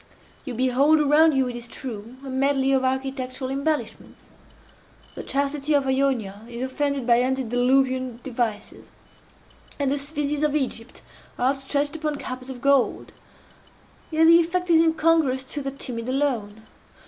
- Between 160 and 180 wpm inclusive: No, average, 145 wpm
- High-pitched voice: Yes, very high, 270 Hz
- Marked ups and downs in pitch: No, narrow, 2.4 semitones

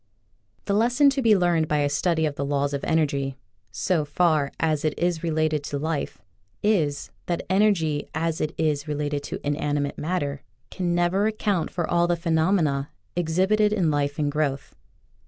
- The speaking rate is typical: Yes, average, 180 wpm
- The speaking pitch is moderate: Yes, medium, 160 Hz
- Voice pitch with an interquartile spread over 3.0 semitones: Yes, average, 3.4 semitones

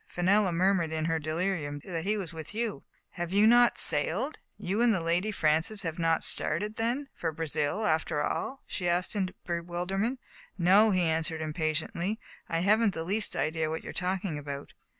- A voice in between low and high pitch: Yes, medium, 175 Hz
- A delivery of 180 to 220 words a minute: Yes, average, 190 wpm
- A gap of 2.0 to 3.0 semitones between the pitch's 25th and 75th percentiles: No, average, 4.2 semitones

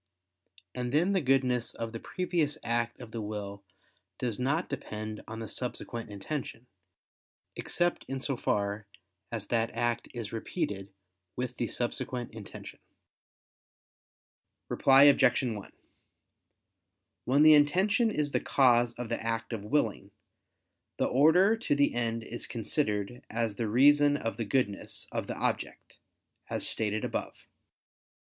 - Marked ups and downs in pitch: No, average, 4.2 semitones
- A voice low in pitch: Yes, low, 120 Hz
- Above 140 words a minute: No, slow, 135 wpm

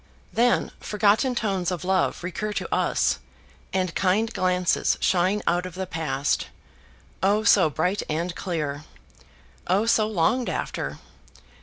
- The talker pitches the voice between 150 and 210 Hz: Yes, medium, 185 Hz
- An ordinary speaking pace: No, slow, 130 wpm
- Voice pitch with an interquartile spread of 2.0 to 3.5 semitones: Yes, average, 3.2 semitones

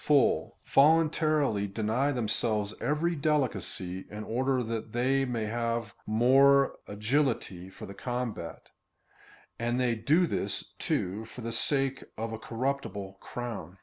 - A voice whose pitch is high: No, low, 120 Hz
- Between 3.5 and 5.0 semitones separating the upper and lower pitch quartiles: Yes, average, 4.2 semitones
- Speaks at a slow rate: Yes, slow, 125 wpm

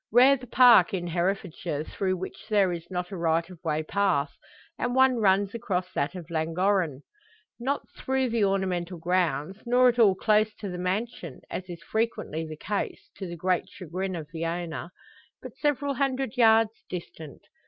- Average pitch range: Yes, average, 4.8 semitones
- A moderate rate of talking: Yes, average, 175 wpm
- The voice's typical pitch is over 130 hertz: Yes, high, 190 Hz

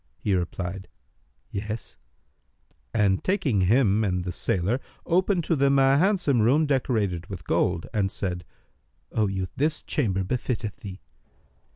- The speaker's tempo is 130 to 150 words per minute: Yes, slow, 135 wpm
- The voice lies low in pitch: Yes, low, 105 Hz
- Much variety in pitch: Yes, wide, 6.4 semitones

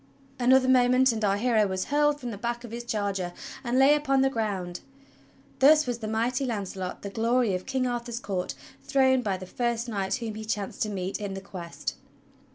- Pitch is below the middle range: No, high, 230 Hz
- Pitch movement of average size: Yes, average, 4.2 semitones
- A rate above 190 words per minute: Yes, average, 200 wpm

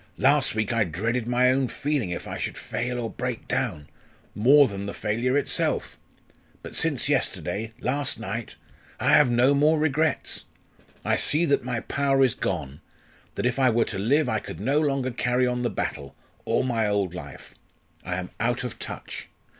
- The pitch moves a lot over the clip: No, average, 4.2 semitones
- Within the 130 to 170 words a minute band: No, average, 180 wpm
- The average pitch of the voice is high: No, low, 125 Hz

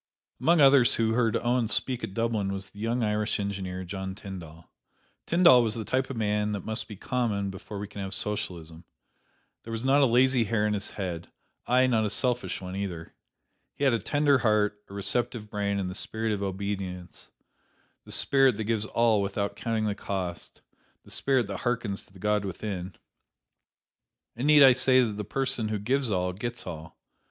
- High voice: No, low, 105 Hz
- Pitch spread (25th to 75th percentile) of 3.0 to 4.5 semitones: Yes, average, 3.6 semitones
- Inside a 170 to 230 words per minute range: Yes, average, 190 wpm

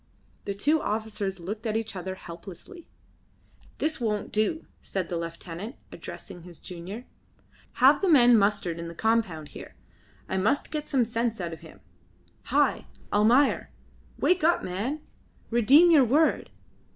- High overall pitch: Yes, high, 215 Hz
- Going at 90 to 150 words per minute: Yes, average, 145 wpm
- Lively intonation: Yes, wide, 6.1 semitones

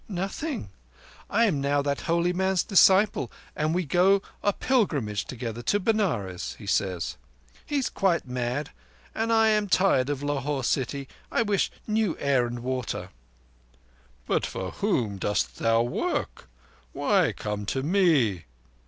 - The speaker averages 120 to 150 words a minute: Yes, average, 140 wpm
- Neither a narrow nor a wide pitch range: No, wide, 8.4 semitones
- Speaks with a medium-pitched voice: Yes, medium, 145 Hz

